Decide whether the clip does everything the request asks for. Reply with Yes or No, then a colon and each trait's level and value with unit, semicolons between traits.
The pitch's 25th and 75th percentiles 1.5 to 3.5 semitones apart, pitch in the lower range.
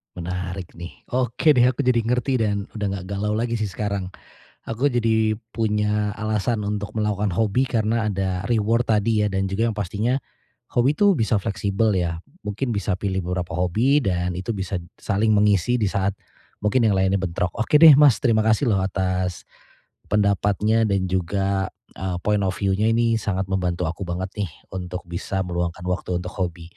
Yes: average, 3.2 semitones; low, 100 Hz